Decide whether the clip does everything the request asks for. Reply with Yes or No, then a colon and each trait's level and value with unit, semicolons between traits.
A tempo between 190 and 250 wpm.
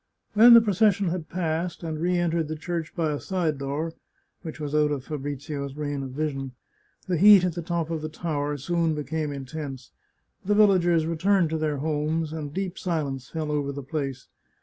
Yes: average, 195 wpm